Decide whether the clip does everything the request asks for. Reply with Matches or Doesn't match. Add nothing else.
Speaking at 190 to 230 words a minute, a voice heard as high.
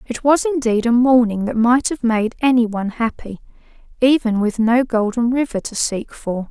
Doesn't match